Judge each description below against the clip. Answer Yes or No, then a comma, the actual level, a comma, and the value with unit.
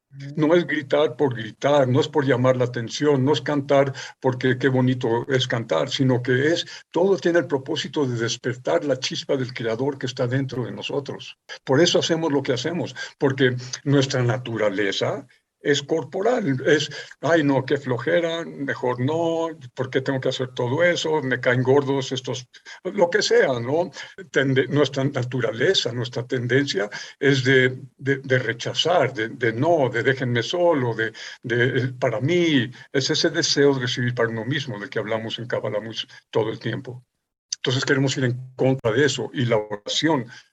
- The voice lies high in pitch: No, low, 135 Hz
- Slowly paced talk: No, average, 175 wpm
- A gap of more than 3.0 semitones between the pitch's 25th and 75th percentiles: No, average, 2.7 semitones